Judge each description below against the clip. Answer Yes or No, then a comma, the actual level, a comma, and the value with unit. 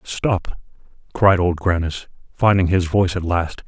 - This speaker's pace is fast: No, average, 145 wpm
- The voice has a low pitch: Yes, very low, 90 Hz